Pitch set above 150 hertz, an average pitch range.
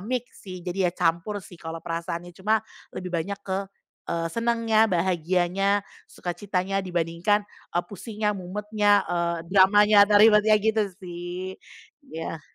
Yes: high, 190 Hz; average, 3.2 semitones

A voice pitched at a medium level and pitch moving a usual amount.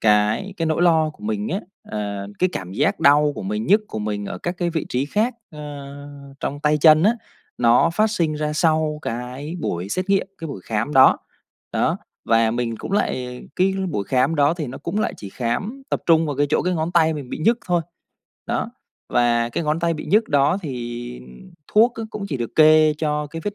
No: medium, 150 Hz; wide, 6.0 semitones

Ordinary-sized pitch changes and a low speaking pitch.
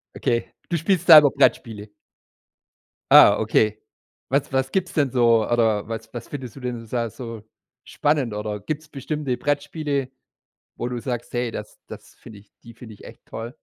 Yes: average, 4.0 semitones; low, 120 Hz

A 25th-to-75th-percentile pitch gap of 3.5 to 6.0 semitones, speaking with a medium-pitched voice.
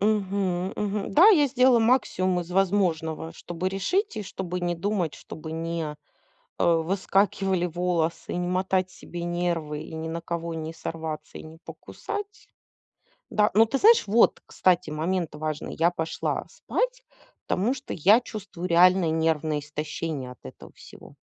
Yes: average, 3.9 semitones; medium, 180 Hz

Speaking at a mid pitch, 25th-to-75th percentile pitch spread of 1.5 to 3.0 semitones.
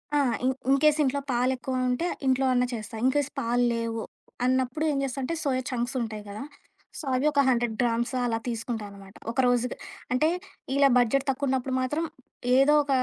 No: very high, 255 Hz; narrow, 2.5 semitones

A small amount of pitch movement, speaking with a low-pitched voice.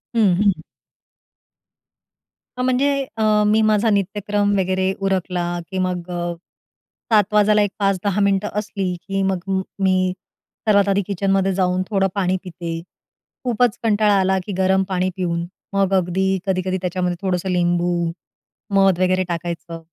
No: narrow, 1.9 semitones; high, 190 Hz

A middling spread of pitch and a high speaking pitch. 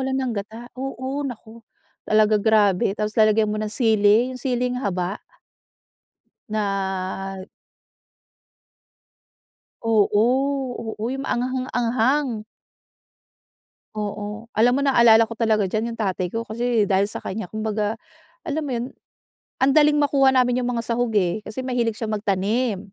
Yes: average, 3.1 semitones; high, 225 Hz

